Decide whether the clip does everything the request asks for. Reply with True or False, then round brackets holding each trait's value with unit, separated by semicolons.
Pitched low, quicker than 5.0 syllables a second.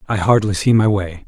True (100 Hz; 5.4 syllables/s)